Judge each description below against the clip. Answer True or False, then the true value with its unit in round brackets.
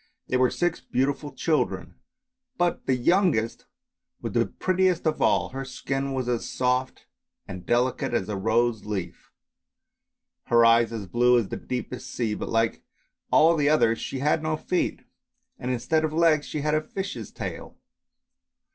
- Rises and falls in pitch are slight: False (5.0 semitones)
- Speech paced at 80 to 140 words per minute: False (160 wpm)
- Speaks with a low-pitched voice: True (130 Hz)